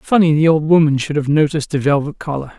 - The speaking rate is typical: No, fast, 230 wpm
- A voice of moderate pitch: Yes, medium, 150 Hz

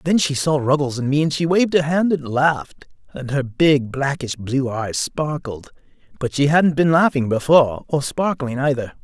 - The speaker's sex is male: Yes, male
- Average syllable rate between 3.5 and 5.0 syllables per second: Yes, 4.8 syllables/s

